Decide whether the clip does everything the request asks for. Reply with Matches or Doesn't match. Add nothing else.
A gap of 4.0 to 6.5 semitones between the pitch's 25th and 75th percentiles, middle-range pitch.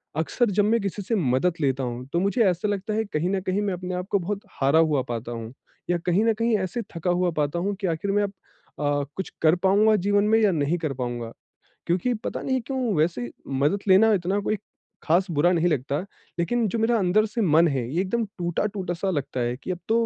Matches